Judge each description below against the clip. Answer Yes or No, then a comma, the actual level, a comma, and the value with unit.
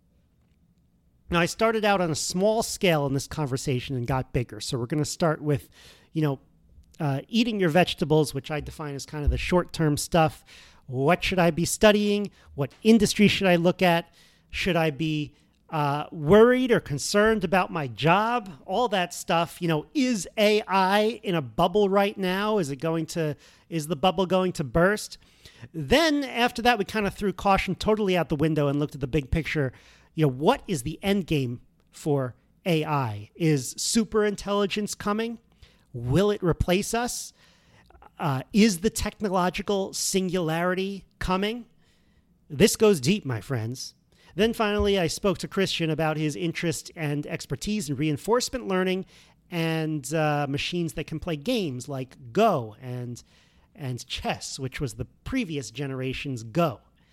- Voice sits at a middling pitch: Yes, medium, 170 Hz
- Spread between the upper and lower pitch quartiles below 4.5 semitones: No, wide, 5.6 semitones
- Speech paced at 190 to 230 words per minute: No, average, 165 wpm